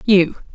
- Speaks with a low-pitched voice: No, high, 190 Hz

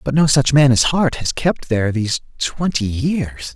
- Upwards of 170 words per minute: Yes, fast, 205 wpm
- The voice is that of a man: Yes, male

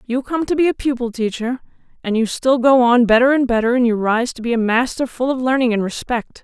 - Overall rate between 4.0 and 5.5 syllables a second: No, 5.8 syllables/s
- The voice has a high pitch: Yes, high, 245 Hz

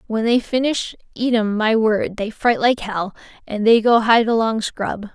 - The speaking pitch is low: No, high, 220 Hz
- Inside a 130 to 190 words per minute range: No, average, 200 wpm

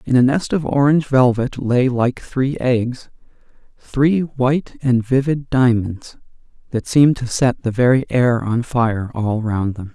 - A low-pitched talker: Yes, low, 125 Hz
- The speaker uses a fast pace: No, average, 165 wpm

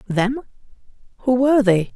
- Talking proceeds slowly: Yes, slow, 125 wpm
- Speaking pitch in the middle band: No, high, 235 Hz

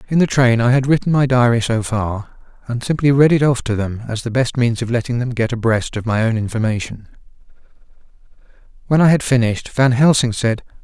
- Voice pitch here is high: No, low, 120 Hz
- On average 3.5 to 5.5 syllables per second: No, 5.7 syllables/s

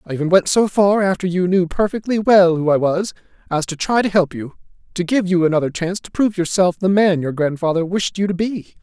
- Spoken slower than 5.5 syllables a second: No, 5.8 syllables/s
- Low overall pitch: No, medium, 180 Hz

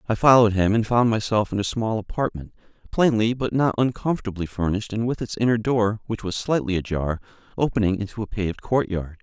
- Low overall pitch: Yes, low, 110 Hz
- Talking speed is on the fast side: No, average, 190 wpm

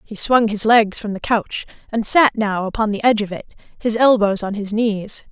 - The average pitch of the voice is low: No, high, 215 Hz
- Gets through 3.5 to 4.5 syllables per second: No, 5.0 syllables/s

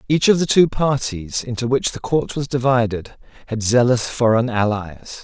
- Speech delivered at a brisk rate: No, average, 170 wpm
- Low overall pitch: Yes, low, 120 Hz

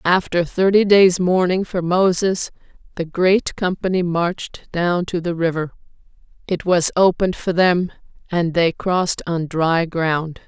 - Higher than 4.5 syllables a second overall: No, 4.2 syllables/s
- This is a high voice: No, medium, 175 Hz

